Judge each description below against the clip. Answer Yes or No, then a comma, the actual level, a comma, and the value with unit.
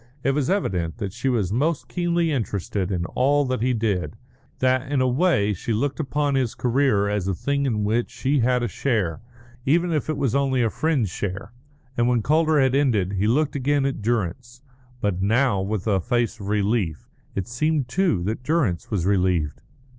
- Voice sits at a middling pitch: No, low, 120 Hz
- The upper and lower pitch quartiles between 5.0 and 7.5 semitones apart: Yes, wide, 5.5 semitones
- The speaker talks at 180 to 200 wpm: Yes, average, 190 wpm